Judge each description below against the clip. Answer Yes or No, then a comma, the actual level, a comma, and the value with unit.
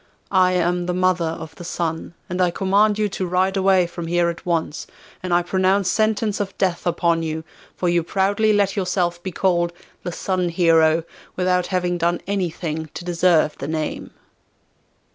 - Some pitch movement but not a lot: No, narrow, 1.8 semitones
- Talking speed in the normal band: Yes, average, 175 wpm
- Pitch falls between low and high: Yes, medium, 175 Hz